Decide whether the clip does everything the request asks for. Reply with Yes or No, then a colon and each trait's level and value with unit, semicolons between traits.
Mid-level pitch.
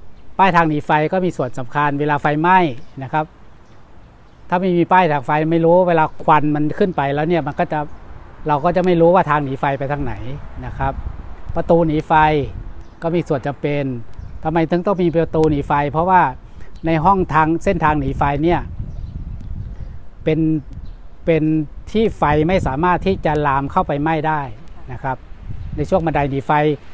Yes: medium, 150 Hz